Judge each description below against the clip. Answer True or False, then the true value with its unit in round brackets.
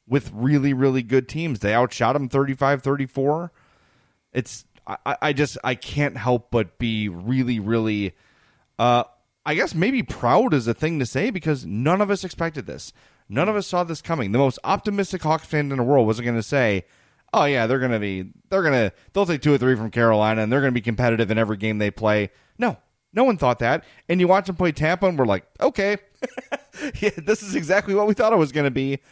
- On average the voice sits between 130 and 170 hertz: True (135 Hz)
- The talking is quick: True (215 wpm)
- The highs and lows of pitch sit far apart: True (6.1 semitones)